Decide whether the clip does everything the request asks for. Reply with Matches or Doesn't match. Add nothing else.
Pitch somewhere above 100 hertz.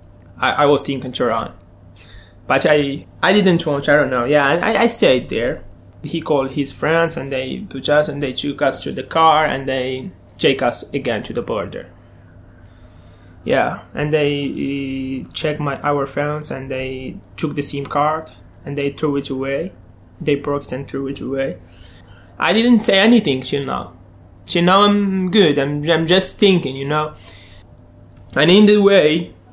Matches